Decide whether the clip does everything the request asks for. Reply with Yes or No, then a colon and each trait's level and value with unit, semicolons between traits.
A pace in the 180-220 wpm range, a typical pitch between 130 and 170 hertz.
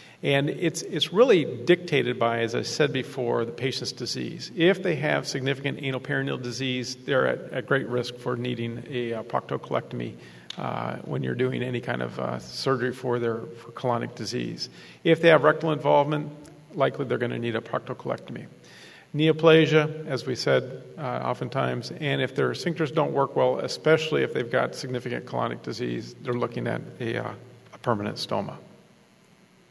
No: average, 165 wpm; low, 135 Hz